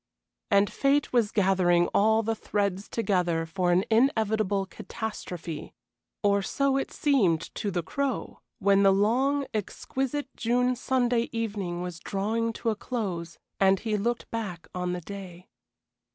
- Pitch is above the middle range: Yes, high, 205 Hz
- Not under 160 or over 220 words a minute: No, average, 140 wpm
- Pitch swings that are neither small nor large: Yes, average, 4.2 semitones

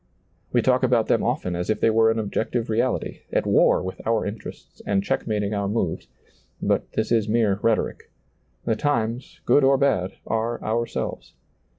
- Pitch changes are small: Yes, narrow, 2.3 semitones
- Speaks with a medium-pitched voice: No, low, 110 Hz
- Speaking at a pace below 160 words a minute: No, average, 170 wpm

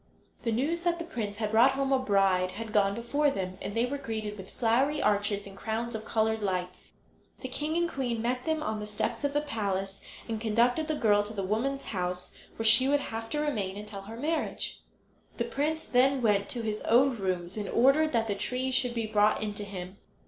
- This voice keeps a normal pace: No, fast, 220 wpm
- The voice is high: Yes, high, 225 Hz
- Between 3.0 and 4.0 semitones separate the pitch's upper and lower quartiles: No, average, 4.6 semitones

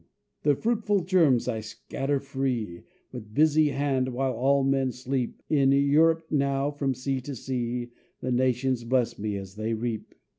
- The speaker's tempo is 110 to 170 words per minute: Yes, average, 155 wpm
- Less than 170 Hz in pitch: Yes, low, 135 Hz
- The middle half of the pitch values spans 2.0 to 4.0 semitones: Yes, narrow, 2.6 semitones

